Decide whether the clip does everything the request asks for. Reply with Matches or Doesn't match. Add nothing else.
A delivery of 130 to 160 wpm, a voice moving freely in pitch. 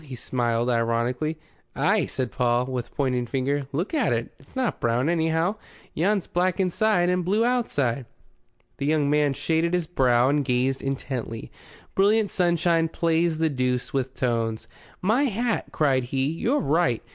Matches